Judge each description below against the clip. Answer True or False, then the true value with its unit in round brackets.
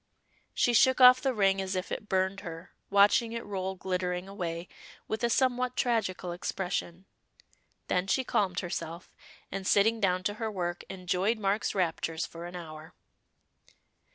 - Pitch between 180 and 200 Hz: True (190 Hz)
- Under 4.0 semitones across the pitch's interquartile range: True (3.3 semitones)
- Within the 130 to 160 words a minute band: True (155 wpm)